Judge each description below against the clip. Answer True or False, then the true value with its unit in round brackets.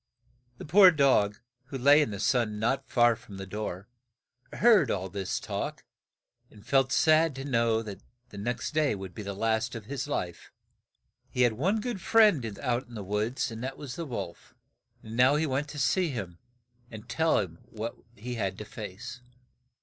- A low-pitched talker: True (120 Hz)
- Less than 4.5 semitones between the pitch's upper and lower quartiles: False (5.2 semitones)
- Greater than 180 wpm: True (190 wpm)